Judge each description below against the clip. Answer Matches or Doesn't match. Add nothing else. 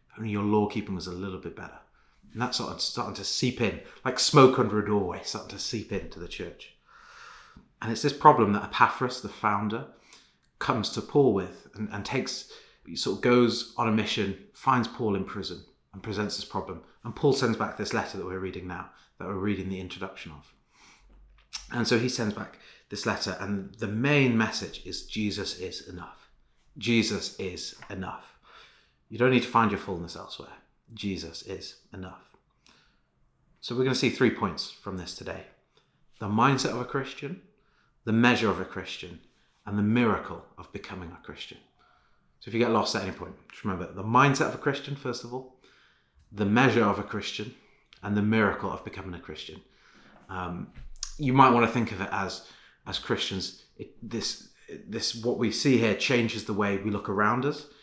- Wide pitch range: Doesn't match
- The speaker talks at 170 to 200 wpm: Matches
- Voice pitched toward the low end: Matches